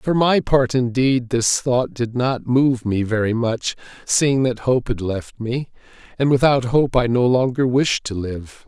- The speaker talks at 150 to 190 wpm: Yes, average, 185 wpm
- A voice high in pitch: No, low, 125 Hz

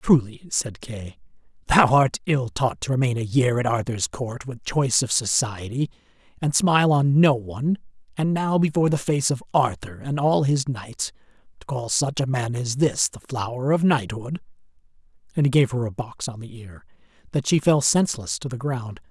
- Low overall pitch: Yes, low, 130 Hz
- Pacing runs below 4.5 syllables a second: No, 5.0 syllables/s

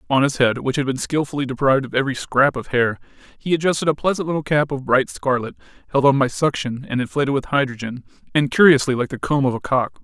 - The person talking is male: Yes, male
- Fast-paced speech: Yes, fast, 225 wpm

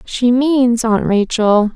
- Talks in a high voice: Yes, high, 235 Hz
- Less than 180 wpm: Yes, slow, 135 wpm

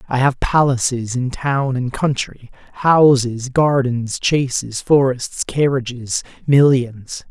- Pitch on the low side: Yes, low, 130 Hz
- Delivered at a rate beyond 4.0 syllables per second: No, 3.5 syllables/s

